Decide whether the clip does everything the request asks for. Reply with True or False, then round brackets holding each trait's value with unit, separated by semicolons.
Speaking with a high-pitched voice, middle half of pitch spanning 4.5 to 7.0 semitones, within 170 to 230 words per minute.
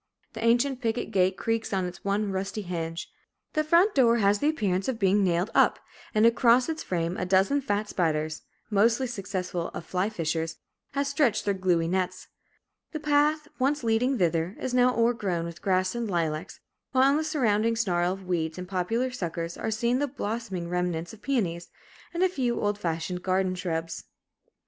True (200 Hz; 5.3 semitones; 180 wpm)